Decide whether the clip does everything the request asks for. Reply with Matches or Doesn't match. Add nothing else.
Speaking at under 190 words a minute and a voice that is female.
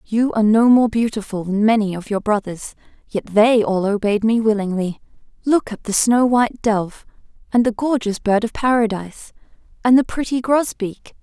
Matches